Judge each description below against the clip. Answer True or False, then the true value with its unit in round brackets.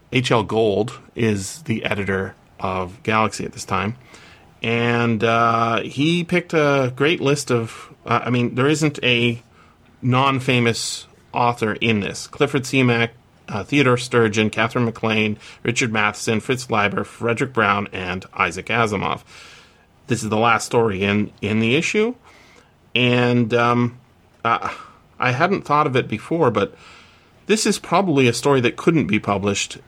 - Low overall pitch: True (115 Hz)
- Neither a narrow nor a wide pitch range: True (3.3 semitones)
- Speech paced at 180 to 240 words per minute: False (145 wpm)